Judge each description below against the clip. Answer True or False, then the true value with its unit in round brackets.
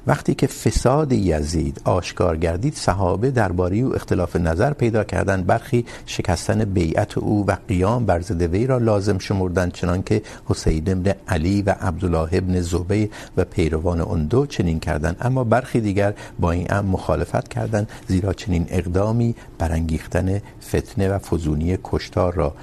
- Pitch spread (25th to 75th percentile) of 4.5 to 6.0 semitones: False (3.9 semitones)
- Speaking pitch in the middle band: False (95 Hz)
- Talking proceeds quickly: False (150 wpm)